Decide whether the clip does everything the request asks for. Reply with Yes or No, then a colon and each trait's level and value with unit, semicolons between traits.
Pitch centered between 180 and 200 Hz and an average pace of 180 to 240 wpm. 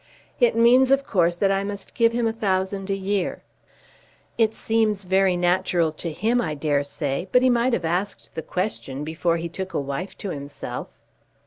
Yes: high, 190 Hz; average, 190 wpm